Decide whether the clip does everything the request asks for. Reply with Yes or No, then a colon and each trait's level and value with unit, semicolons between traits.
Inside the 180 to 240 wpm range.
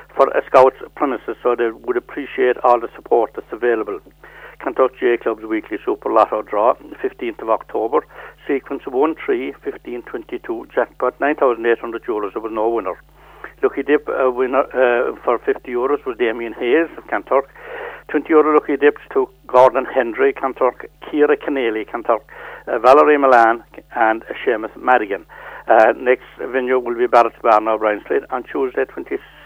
No: average, 155 wpm